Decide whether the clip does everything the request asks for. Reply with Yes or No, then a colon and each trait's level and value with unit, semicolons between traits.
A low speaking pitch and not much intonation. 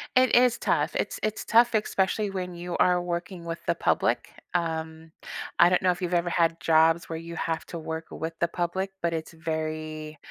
No: medium, 170 Hz; narrow, 2.0 semitones